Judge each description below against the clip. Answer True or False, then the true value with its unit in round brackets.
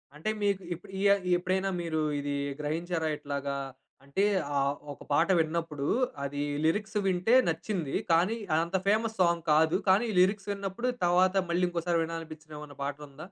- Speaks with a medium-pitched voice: True (170 Hz)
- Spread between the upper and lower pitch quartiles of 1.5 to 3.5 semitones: False (4.0 semitones)